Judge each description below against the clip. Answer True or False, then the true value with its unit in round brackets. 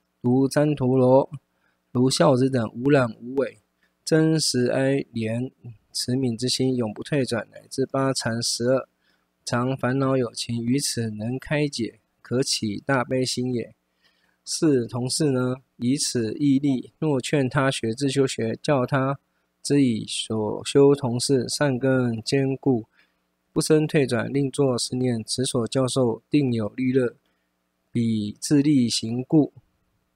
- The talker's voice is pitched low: True (125 Hz)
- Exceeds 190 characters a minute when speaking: False (185 characters per minute)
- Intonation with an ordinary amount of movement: True (3.2 semitones)